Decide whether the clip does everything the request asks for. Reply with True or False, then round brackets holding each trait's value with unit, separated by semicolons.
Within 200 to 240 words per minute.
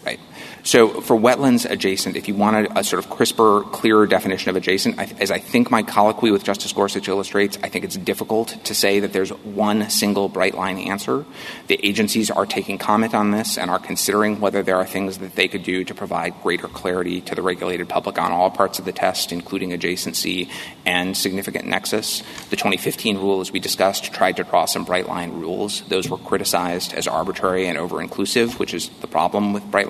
True (205 wpm)